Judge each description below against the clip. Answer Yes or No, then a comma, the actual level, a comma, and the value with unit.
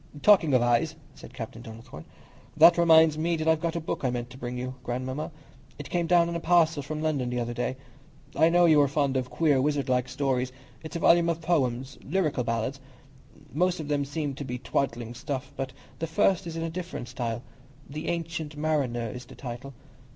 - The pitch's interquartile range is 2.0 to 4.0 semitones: No, average, 4.4 semitones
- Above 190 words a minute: Yes, average, 200 wpm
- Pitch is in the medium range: Yes, medium, 145 Hz